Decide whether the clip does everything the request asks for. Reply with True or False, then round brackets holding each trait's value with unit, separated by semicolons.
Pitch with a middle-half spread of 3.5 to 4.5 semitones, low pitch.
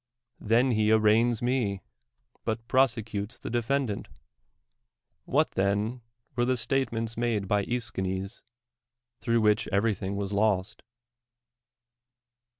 False (2.9 semitones; 110 Hz)